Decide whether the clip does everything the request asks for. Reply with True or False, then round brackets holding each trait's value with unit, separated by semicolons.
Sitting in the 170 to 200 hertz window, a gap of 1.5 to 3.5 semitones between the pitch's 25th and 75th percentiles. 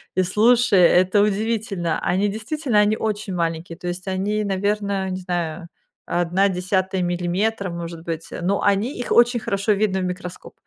True (190 Hz; 3.0 semitones)